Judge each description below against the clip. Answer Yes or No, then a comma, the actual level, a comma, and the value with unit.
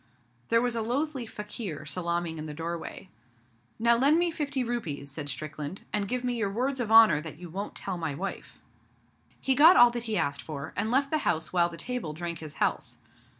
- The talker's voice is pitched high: Yes, high, 200 Hz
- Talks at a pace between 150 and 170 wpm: No, fast, 205 wpm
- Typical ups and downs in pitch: No, wide, 7.2 semitones